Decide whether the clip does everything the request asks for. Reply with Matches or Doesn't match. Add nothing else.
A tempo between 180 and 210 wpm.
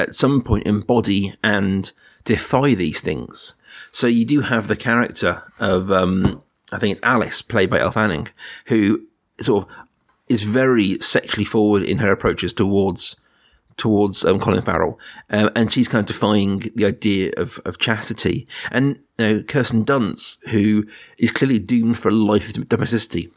Doesn't match